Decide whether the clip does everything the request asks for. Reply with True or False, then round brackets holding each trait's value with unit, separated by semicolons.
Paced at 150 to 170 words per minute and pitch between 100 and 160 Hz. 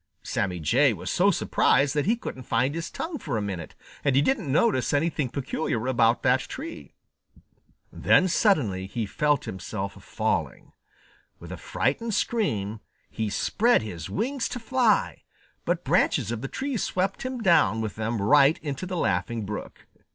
True (160 wpm; 135 Hz)